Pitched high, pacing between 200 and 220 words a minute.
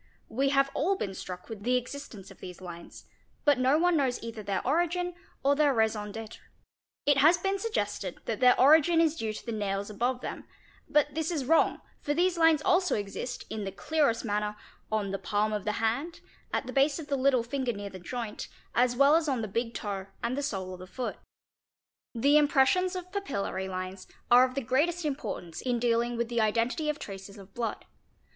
Yes: high, 245 Hz; fast, 205 wpm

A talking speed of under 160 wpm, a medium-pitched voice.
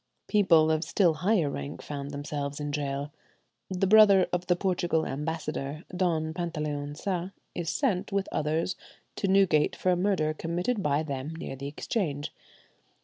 Yes: average, 150 wpm; medium, 160 Hz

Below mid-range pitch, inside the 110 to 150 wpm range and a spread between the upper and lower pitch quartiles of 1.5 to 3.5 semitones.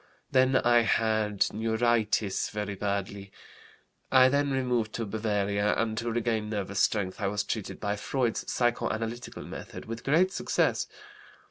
Yes: low, 110 Hz; slow, 135 wpm; narrow, 2.6 semitones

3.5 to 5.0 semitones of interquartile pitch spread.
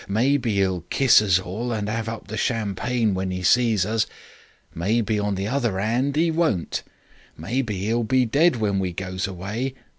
Yes: average, 4.1 semitones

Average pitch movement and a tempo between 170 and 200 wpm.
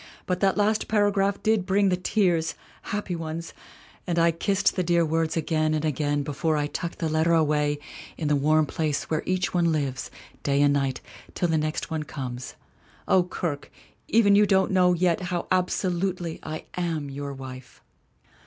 Yes: average, 3.5 semitones; average, 175 wpm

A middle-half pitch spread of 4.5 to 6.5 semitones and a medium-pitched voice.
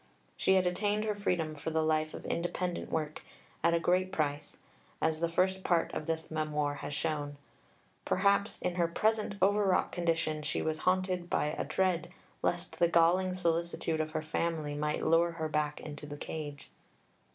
No: average, 2.8 semitones; medium, 165 Hz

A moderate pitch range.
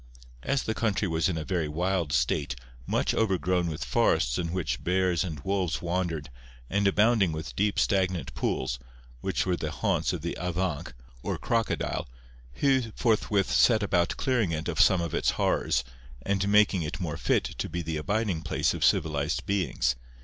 Yes: average, 4.1 semitones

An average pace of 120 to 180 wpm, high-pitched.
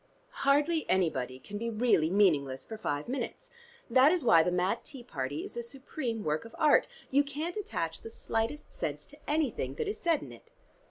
No: average, 195 wpm; high, 230 Hz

